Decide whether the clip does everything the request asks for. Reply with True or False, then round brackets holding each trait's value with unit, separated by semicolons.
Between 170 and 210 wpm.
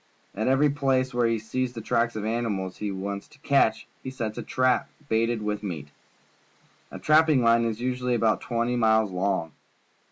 True (185 wpm)